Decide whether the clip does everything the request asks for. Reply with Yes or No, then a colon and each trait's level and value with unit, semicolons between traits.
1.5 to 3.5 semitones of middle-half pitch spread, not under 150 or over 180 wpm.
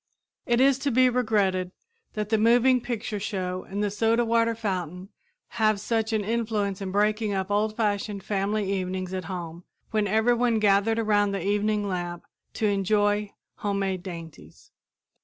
Yes: narrow, 2.5 semitones; average, 155 wpm